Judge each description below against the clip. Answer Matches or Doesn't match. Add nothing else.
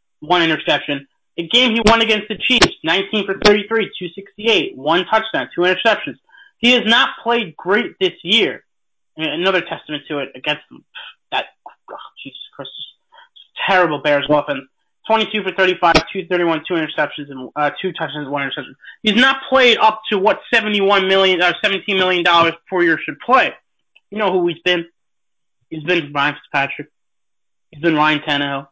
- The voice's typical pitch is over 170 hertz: Matches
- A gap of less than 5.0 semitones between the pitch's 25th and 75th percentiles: Doesn't match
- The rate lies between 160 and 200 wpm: Matches